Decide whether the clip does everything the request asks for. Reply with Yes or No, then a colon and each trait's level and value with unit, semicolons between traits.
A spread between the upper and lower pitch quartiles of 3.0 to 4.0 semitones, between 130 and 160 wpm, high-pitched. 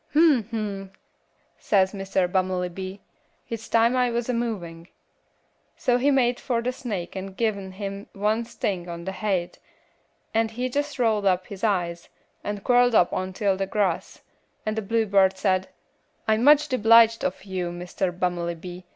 Yes: average, 3.7 semitones; average, 155 wpm; high, 200 Hz